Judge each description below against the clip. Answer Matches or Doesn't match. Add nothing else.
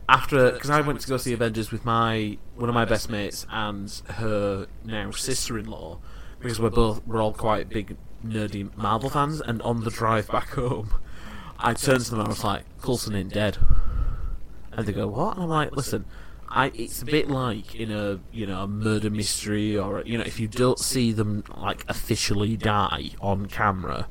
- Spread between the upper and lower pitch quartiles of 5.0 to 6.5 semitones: Doesn't match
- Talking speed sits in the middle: Matches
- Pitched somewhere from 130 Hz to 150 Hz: Doesn't match